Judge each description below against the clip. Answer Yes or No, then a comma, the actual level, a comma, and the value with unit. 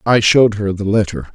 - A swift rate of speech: Yes, fast, 225 wpm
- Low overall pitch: Yes, low, 105 Hz